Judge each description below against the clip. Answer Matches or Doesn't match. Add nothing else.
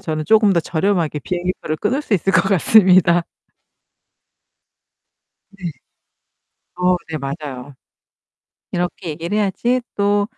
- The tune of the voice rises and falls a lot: Doesn't match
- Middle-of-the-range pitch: Matches